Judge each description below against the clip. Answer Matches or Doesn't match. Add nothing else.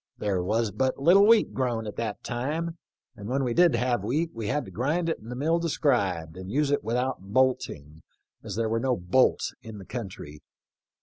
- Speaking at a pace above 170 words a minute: Matches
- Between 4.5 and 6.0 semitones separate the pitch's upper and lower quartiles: Matches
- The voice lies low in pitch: Matches